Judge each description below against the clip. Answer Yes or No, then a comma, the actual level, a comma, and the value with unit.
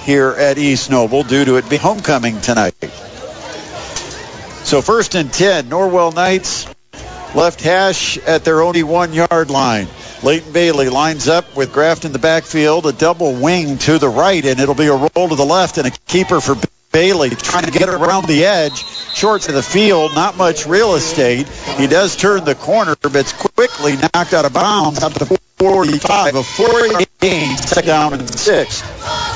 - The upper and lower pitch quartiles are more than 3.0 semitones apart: Yes, average, 4.4 semitones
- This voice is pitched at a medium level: Yes, medium, 160 Hz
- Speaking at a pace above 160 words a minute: Yes, average, 180 wpm